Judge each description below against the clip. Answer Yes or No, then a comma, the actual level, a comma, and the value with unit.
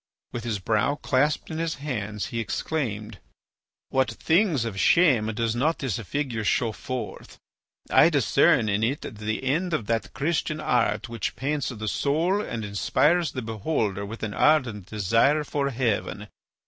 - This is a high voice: No, low, 120 Hz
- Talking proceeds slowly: No, average, 155 wpm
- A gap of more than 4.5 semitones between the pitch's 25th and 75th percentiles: Yes, wide, 5.5 semitones